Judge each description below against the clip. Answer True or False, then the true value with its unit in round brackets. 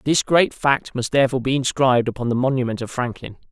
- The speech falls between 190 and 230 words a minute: True (205 wpm)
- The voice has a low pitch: True (130 Hz)